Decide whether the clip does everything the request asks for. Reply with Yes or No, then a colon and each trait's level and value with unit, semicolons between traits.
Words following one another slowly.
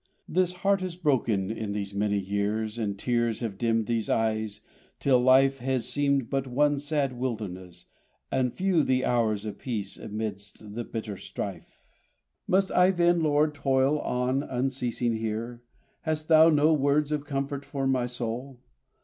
No: average, 155 wpm